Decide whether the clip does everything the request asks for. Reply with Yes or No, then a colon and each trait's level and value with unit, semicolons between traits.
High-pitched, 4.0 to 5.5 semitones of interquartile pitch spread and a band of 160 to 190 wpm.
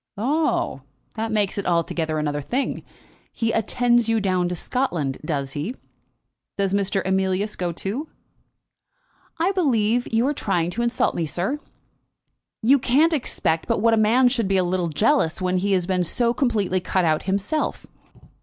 Yes: high, 200 Hz; average, 5.2 semitones; average, 165 wpm